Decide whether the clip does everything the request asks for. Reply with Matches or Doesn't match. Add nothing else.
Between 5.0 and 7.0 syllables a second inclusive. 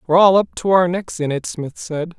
Matches